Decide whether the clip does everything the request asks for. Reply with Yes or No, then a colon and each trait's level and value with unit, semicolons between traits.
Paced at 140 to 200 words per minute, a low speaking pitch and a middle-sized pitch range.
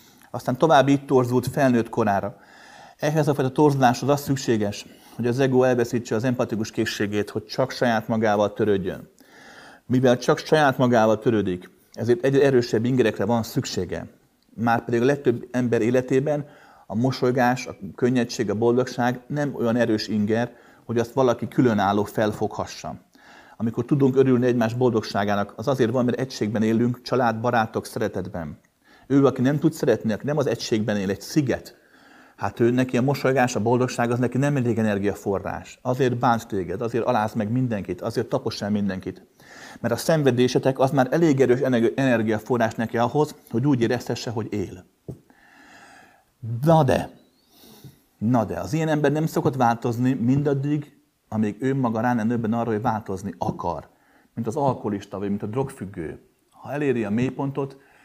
Yes: fast, 155 wpm; low, 120 Hz; average, 3.3 semitones